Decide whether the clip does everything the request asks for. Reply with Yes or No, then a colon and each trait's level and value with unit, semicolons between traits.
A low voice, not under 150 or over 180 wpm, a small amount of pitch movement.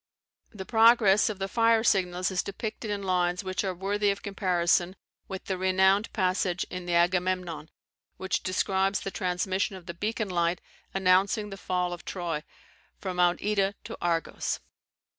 No: high, 190 Hz; average, 160 wpm; narrow, 1.9 semitones